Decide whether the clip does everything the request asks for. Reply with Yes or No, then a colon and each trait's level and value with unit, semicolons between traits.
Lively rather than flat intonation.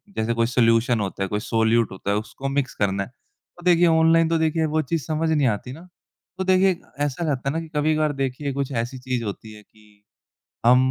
Yes: wide, 5.9 semitones